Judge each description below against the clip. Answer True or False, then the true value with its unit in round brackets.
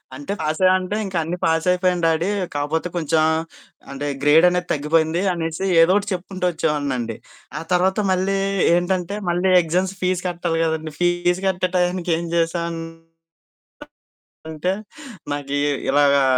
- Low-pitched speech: False (170 Hz)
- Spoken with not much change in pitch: True (2.2 semitones)